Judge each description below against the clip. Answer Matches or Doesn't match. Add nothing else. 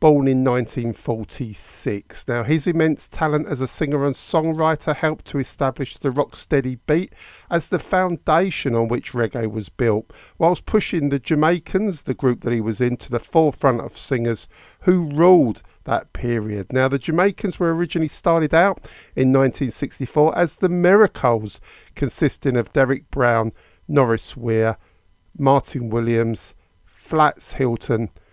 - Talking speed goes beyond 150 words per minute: Doesn't match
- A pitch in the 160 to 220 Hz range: Doesn't match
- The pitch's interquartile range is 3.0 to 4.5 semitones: Doesn't match